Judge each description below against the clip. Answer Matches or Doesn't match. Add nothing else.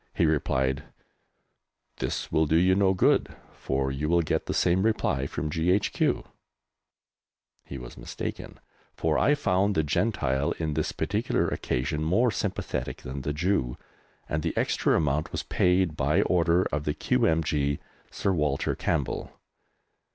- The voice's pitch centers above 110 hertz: Doesn't match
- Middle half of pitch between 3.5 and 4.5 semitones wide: Matches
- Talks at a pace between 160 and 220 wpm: Doesn't match